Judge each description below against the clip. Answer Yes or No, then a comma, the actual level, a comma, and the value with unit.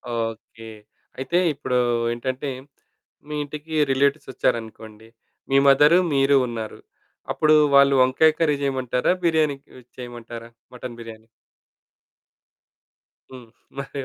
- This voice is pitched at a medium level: No, low, 130 Hz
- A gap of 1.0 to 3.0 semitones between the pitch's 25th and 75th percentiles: No, average, 3.4 semitones